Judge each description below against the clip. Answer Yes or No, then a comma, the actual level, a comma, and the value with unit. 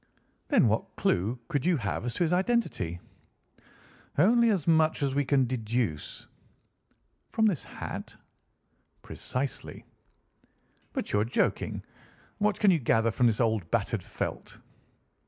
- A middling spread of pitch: No, wide, 7.8 semitones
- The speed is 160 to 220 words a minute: No, slow, 135 wpm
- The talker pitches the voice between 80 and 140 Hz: Yes, low, 135 Hz